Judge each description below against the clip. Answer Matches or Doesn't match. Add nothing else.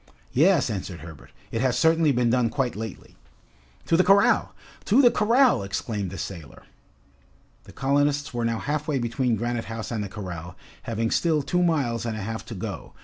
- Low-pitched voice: Matches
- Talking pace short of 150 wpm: Doesn't match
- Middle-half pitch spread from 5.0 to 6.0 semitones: Matches